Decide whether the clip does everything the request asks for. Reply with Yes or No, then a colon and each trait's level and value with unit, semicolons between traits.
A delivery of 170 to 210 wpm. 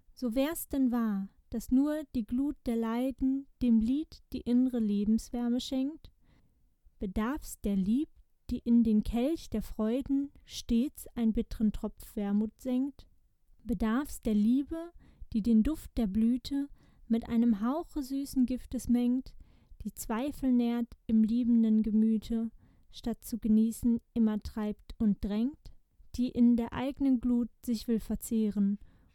No: average, 135 wpm